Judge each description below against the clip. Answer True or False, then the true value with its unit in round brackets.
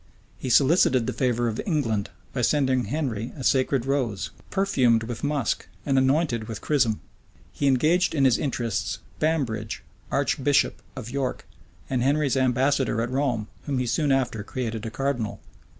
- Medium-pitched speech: False (130 Hz)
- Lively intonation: False (3.4 semitones)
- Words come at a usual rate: True (150 wpm)